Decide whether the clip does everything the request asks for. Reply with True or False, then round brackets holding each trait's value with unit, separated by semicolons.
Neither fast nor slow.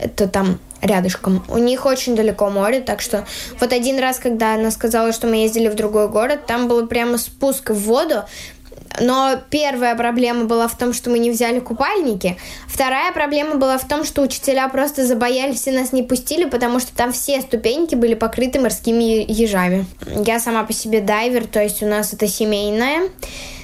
False (185 wpm)